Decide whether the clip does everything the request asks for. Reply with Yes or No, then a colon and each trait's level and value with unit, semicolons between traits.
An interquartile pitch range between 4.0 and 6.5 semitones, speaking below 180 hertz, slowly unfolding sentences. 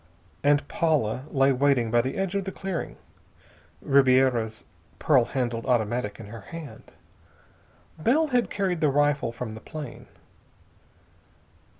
Yes: average, 5.2 semitones; low, 135 Hz; slow, 125 wpm